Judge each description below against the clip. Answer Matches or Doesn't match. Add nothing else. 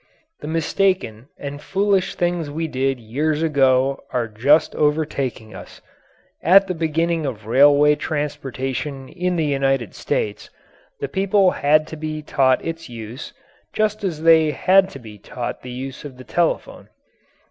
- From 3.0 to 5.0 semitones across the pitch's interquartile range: Matches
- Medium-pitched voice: Matches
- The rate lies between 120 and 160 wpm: Matches